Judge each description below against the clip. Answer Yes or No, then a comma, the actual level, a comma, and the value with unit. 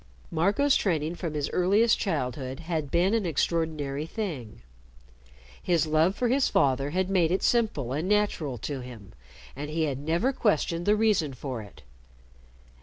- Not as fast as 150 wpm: No, average, 155 wpm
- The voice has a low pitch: No, medium, 160 Hz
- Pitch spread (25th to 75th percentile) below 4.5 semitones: No, wide, 5.5 semitones